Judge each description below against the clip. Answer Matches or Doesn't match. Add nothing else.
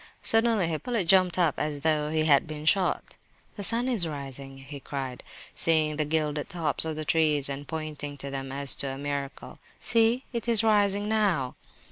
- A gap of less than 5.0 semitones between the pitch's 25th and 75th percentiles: Doesn't match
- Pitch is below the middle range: Doesn't match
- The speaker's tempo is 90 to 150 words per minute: Doesn't match